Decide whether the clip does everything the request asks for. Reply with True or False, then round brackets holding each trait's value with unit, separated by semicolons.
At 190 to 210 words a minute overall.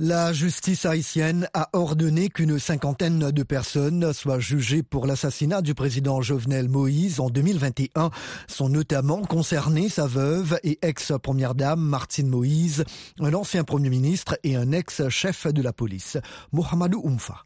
False (145 wpm)